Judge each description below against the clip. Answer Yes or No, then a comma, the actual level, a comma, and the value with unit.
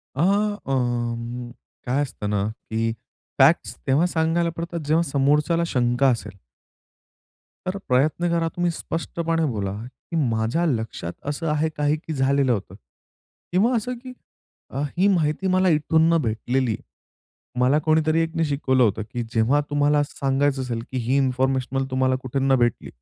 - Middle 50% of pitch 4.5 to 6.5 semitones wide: Yes, average, 4.9 semitones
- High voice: No, low, 135 Hz